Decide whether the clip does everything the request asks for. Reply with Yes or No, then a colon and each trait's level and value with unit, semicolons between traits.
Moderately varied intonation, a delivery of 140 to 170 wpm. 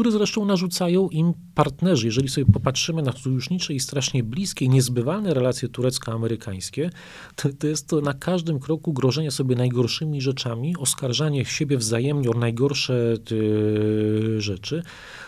No: average, 4.7 semitones; average, 130 wpm